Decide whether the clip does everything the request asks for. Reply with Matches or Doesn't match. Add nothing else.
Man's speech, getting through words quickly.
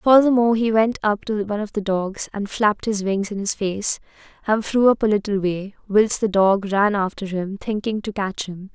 Doesn't match